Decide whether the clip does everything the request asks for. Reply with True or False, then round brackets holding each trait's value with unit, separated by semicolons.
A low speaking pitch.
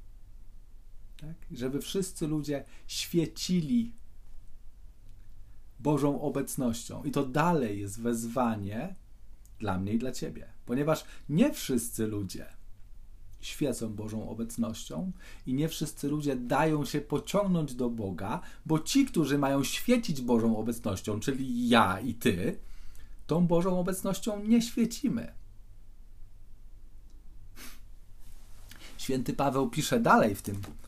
True (115 Hz)